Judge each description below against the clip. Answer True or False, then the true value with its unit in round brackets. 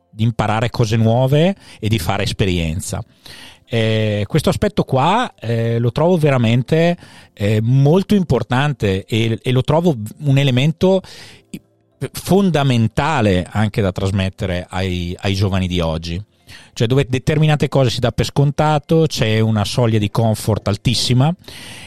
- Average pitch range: False (5.8 semitones)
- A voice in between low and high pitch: False (120 Hz)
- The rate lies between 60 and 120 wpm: False (130 wpm)